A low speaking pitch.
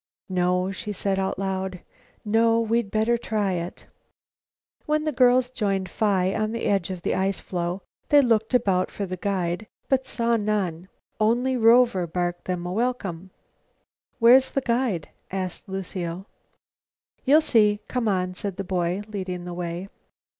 No: high, 195 Hz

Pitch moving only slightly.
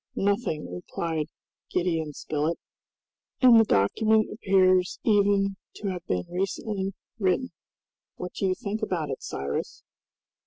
No: average, 4.0 semitones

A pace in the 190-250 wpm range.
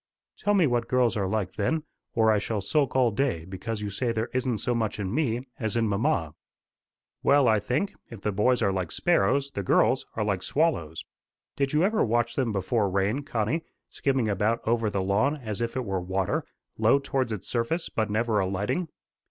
Yes: average, 200 wpm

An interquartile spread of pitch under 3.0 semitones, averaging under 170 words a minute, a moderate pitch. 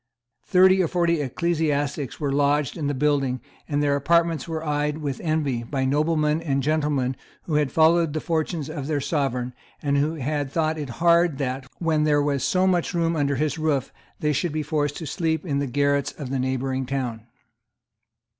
No: narrow, 2.6 semitones; average, 185 wpm; medium, 150 Hz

